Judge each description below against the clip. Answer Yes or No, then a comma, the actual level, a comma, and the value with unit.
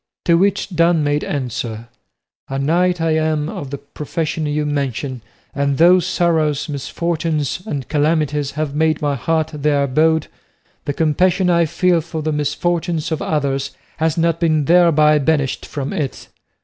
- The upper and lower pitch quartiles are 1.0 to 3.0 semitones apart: Yes, narrow, 2.6 semitones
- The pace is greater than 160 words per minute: No, average, 150 wpm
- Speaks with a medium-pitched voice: Yes, medium, 155 Hz